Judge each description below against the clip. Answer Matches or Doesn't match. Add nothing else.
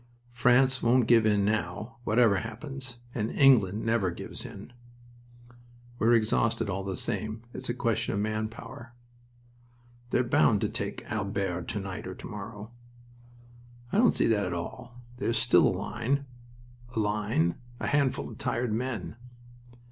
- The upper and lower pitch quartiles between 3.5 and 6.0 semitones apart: Doesn't match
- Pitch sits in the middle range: Doesn't match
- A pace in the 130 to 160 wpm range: Matches